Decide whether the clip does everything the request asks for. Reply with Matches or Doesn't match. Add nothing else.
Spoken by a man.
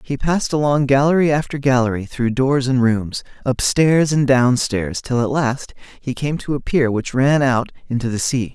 Matches